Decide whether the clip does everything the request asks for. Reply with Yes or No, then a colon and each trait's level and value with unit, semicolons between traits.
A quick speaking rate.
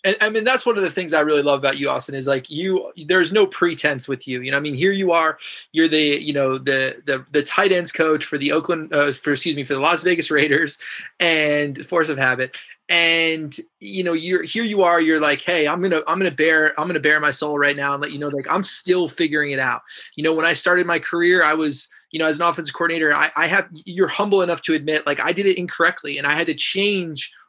Yes: fast, 260 wpm